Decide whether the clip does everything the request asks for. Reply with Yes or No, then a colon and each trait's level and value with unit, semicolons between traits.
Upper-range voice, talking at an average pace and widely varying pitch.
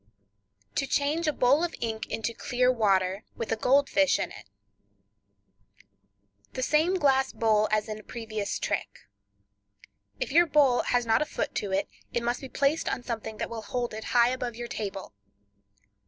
No: high, 240 Hz; average, 165 wpm; average, 4.0 semitones